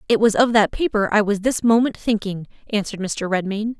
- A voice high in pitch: Yes, high, 210 Hz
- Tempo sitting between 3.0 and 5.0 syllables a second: No, 5.7 syllables/s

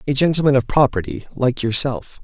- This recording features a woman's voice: No, male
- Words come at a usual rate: Yes, average, 160 wpm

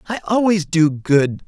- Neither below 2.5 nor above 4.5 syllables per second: Yes, 4.0 syllables/s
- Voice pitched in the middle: Yes, medium, 175 Hz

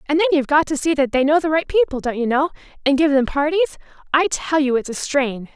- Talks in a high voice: Yes, very high, 290 Hz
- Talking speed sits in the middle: No, fast, 240 wpm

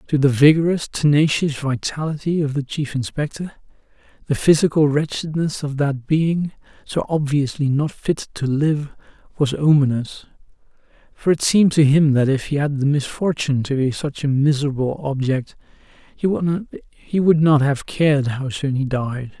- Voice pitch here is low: No, medium, 145 Hz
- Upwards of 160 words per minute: No, average, 150 wpm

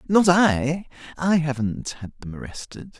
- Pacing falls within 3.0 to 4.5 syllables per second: Yes, 4.2 syllables/s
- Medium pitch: Yes, medium, 155 Hz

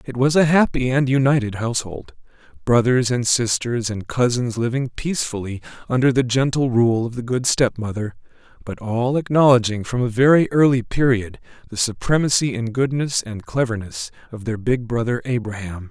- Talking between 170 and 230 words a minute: No, average, 155 wpm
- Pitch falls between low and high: No, low, 120 Hz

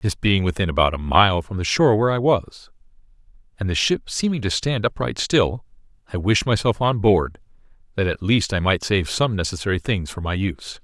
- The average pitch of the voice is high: No, low, 100 Hz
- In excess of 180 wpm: Yes, fast, 205 wpm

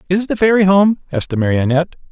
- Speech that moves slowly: No, average, 200 wpm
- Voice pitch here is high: No, medium, 175 Hz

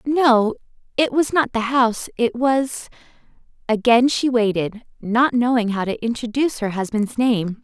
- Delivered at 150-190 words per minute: No, average, 140 wpm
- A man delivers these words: No, female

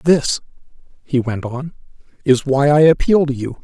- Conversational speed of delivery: Yes, average, 165 wpm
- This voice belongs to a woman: No, male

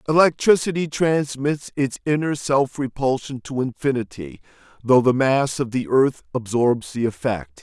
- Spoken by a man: Yes, male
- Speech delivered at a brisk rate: No, slow, 135 wpm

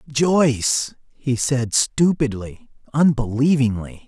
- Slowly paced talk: Yes, slow, 75 wpm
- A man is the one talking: Yes, male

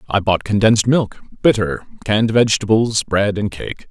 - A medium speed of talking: Yes, average, 155 wpm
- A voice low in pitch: Yes, low, 105 Hz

